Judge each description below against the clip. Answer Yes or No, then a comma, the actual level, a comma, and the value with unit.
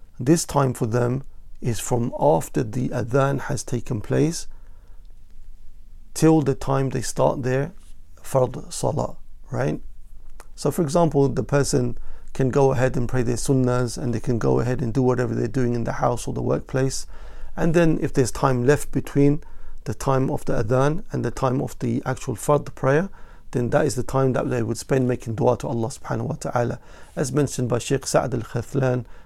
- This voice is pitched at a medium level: No, low, 130 Hz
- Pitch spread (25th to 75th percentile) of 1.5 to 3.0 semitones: Yes, narrow, 2.5 semitones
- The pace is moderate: Yes, average, 190 wpm